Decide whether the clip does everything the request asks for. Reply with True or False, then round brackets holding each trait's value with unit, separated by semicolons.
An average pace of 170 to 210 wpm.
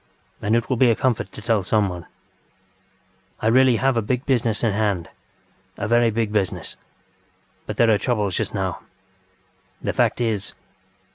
False (160 wpm)